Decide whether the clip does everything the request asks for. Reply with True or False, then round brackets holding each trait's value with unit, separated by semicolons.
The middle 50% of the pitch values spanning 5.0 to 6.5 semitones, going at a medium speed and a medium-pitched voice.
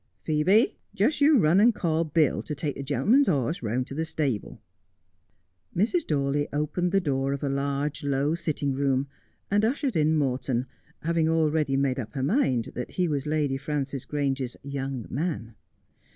False (3.5 semitones; 175 wpm; 145 Hz)